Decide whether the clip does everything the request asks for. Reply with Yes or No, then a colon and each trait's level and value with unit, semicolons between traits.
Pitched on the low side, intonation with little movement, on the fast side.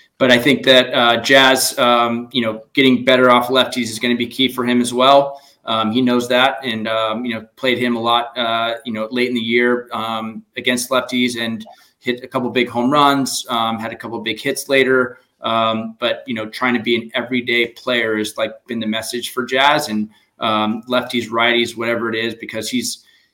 Yes: low, 120 Hz; narrow, 1.9 semitones; fast, 215 wpm